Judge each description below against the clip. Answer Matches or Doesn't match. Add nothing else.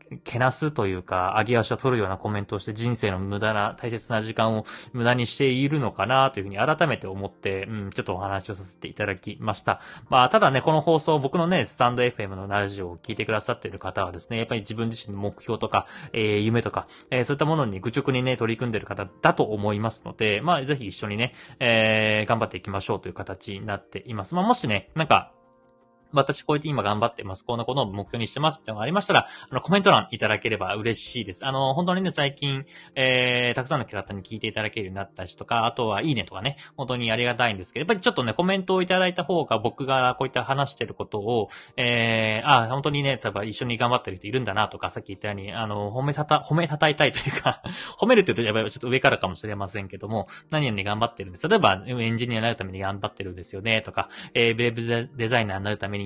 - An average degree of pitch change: Matches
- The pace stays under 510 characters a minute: Doesn't match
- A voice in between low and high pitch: Doesn't match